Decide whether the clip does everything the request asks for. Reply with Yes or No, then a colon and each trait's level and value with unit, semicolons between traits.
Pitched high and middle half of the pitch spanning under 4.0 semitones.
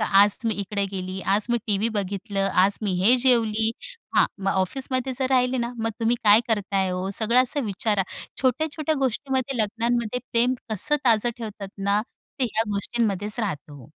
Yes: high, 220 Hz; average, 3.6 semitones